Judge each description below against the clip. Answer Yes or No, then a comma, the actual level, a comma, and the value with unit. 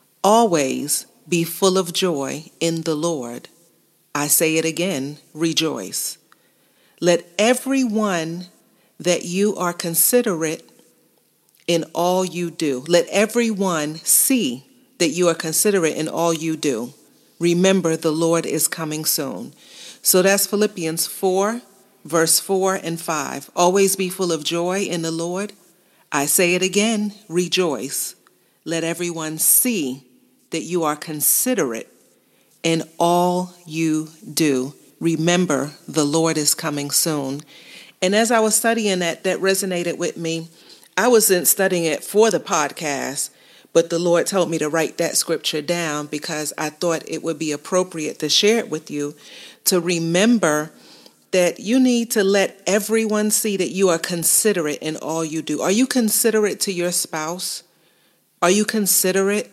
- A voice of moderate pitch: Yes, medium, 175 Hz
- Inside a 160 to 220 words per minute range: No, average, 145 wpm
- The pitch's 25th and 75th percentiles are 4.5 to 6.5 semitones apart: No, average, 3.4 semitones